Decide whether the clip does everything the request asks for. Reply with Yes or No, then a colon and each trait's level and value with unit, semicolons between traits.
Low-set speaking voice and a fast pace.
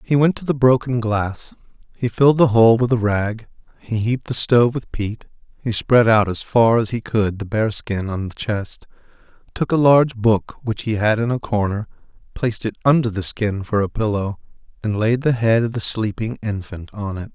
Yes: low, 110 Hz; fast, 210 wpm